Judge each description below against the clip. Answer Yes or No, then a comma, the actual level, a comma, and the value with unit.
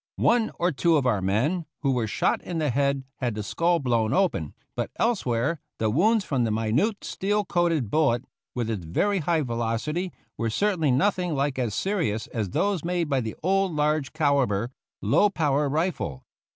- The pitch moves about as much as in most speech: No, wide, 7.1 semitones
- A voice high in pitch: No, medium, 145 Hz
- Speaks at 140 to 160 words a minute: No, average, 180 wpm